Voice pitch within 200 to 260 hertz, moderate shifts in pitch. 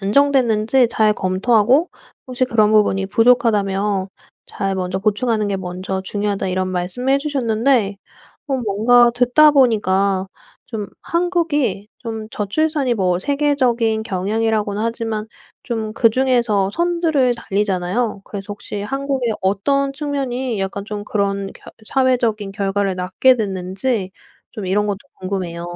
Yes: high, 215 Hz; average, 4.4 semitones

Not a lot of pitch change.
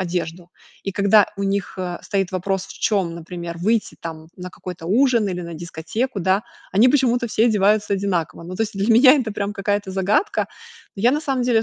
No: average, 3.8 semitones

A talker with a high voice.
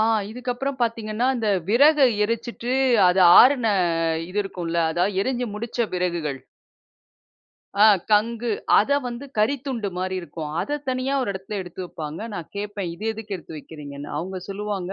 Yes: high, 210 Hz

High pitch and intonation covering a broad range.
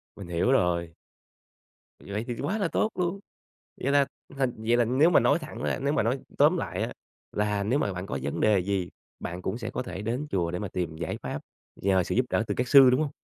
No: low, 110 Hz; wide, 6.4 semitones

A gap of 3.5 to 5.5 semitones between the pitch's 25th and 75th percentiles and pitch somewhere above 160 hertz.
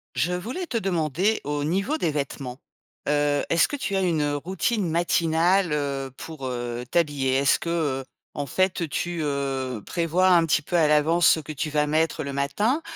No: average, 3.8 semitones; medium, 155 Hz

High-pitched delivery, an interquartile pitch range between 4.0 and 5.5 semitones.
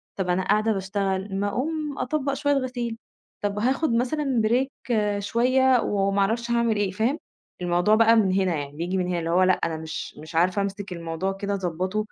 Yes: high, 205 Hz; average, 4.5 semitones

